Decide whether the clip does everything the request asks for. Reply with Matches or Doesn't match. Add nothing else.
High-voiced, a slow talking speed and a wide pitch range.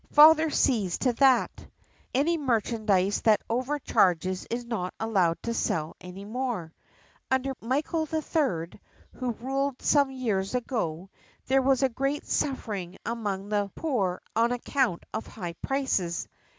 Matches